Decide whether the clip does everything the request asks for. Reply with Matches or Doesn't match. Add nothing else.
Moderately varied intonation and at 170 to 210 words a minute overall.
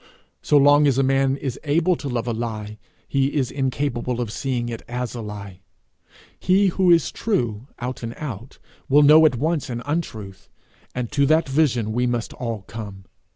Matches